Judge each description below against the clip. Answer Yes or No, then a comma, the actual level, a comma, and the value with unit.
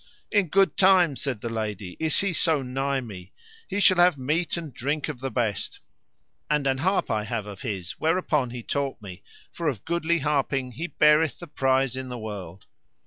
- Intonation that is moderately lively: No, wide, 5.8 semitones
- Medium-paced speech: Yes, average, 195 wpm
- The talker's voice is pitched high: No, low, 135 Hz